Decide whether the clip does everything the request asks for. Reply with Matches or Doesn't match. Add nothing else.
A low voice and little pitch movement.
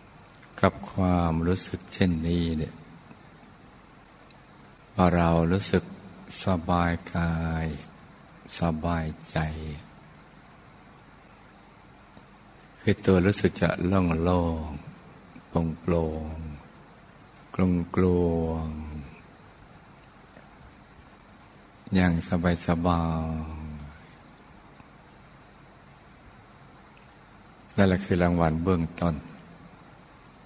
Matches